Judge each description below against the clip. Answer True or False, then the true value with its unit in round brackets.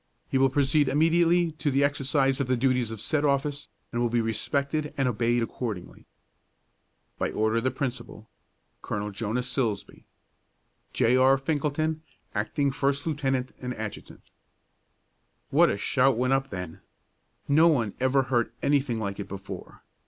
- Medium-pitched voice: False (130 Hz)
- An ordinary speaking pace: True (150 wpm)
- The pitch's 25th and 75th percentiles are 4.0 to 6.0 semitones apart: False (3.6 semitones)